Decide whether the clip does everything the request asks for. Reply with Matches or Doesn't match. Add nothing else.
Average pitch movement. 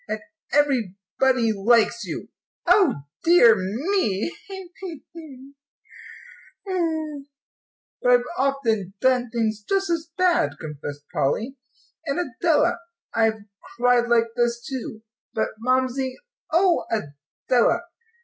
Doesn't match